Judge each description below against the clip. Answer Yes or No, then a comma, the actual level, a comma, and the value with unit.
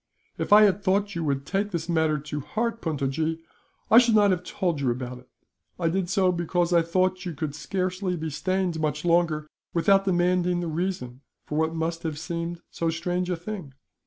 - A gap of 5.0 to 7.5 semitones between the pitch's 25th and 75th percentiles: No, average, 2.9 semitones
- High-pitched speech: No, medium, 170 Hz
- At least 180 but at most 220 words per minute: Yes, average, 195 wpm